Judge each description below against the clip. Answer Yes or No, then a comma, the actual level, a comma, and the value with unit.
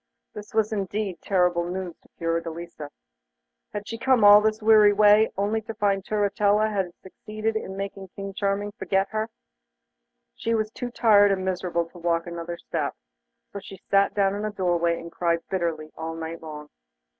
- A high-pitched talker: Yes, high, 195 Hz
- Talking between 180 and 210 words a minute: No, average, 170 wpm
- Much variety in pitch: No, average, 3.6 semitones